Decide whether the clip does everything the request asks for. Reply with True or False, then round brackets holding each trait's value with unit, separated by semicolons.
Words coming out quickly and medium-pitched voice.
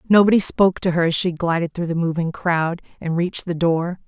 True (220 wpm; 170 Hz)